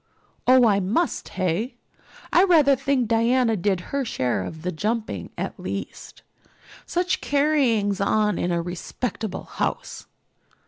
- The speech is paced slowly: Yes, slow, 130 wpm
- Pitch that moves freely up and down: Yes, wide, 6.3 semitones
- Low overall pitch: No, high, 225 Hz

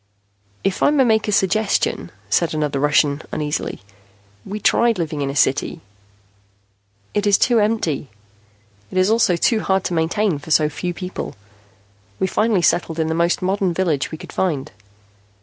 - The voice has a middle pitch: Yes, medium, 180 Hz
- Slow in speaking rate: No, average, 165 wpm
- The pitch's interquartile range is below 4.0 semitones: No, average, 5.0 semitones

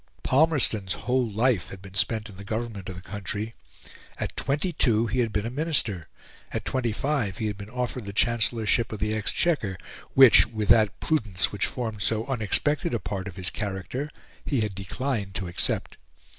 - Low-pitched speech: Yes, low, 110 Hz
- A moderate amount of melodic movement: Yes, average, 3.9 semitones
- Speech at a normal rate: Yes, average, 185 wpm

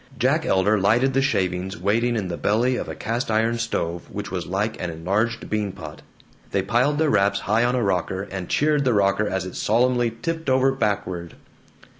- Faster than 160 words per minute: Yes, average, 195 wpm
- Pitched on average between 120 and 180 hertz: No, low, 110 Hz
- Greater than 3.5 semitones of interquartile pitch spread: Yes, average, 4.4 semitones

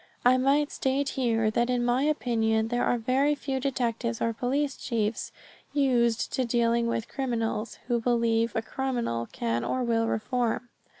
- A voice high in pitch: Yes, high, 240 Hz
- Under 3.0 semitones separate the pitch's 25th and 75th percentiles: Yes, narrow, 2.4 semitones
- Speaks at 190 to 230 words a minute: No, average, 160 wpm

